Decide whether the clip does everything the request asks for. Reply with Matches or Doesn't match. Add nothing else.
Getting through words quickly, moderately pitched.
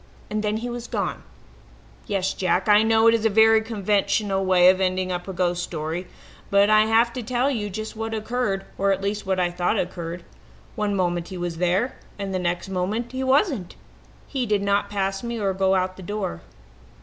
Doesn't match